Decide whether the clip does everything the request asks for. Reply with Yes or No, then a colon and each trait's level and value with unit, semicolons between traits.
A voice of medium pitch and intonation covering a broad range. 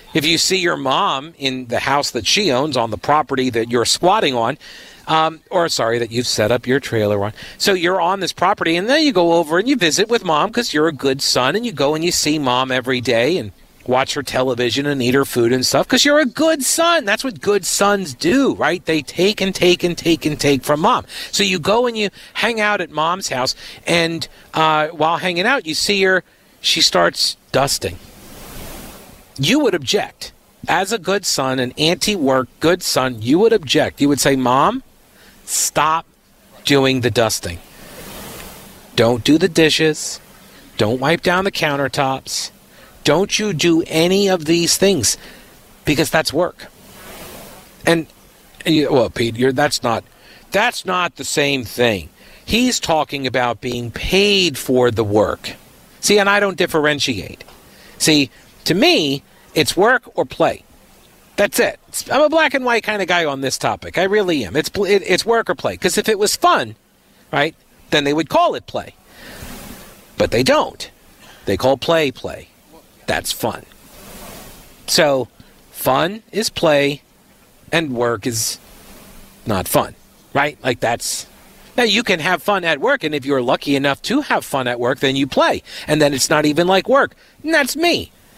Yes: medium, 155 Hz; wide, 6.6 semitones